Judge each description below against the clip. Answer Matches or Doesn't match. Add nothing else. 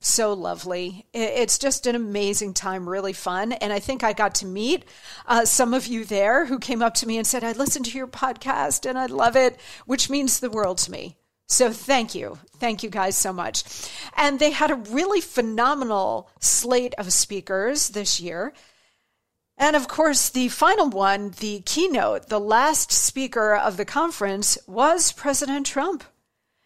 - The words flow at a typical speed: Matches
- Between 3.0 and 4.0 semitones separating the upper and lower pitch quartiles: Doesn't match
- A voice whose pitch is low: Doesn't match